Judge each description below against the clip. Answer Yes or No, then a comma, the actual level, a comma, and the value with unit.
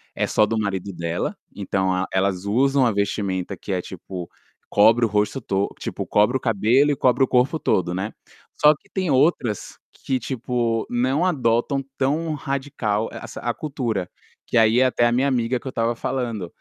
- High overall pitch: No, low, 115 Hz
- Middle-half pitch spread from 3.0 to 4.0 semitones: No, average, 4.7 semitones